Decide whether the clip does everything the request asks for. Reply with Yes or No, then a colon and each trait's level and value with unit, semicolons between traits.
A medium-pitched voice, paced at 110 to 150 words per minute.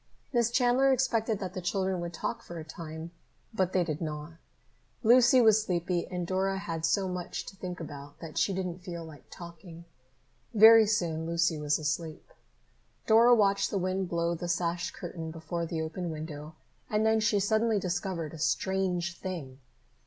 No: medium, 175 Hz; average, 170 wpm